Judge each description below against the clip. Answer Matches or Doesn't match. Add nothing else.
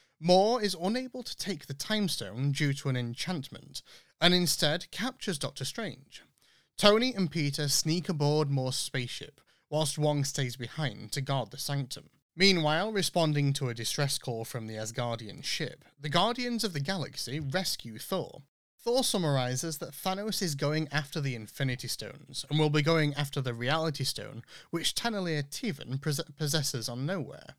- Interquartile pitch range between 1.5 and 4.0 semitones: Doesn't match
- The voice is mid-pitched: Matches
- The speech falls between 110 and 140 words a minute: Doesn't match